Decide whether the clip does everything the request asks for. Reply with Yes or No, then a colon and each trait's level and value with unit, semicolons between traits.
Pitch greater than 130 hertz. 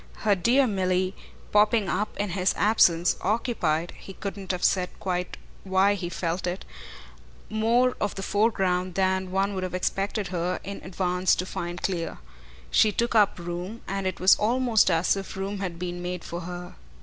Yes: high, 190 Hz